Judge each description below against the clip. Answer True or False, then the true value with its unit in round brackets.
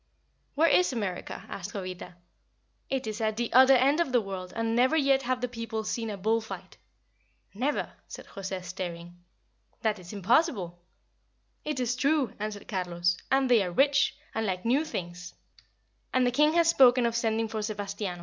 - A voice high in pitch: True (225 Hz)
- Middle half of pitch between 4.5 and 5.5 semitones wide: True (5.1 semitones)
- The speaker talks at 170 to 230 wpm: True (175 wpm)